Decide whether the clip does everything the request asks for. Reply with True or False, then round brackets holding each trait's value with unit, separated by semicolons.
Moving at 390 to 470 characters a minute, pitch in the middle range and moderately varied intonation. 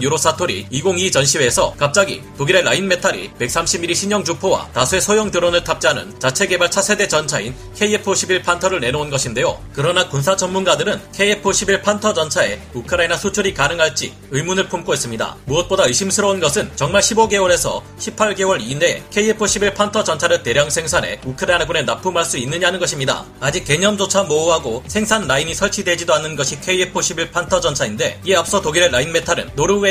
True (405 characters per minute; 180 Hz; 4.3 semitones)